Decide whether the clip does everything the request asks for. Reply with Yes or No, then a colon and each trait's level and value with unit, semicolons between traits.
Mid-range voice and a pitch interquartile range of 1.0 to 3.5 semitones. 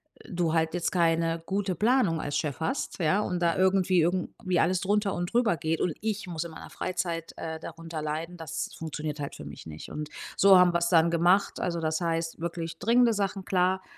Yes: medium, 170 Hz; narrow, 2.5 semitones